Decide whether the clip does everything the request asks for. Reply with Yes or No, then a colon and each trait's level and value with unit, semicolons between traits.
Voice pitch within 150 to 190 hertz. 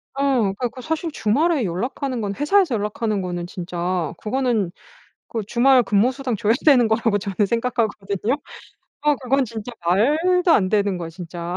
No: high, 225 Hz